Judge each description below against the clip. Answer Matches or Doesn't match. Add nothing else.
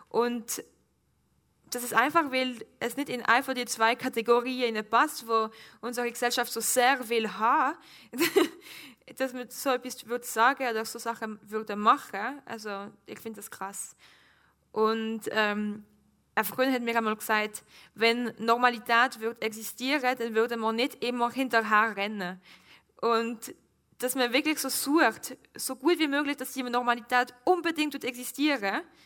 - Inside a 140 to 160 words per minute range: Matches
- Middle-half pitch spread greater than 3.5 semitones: Doesn't match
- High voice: Matches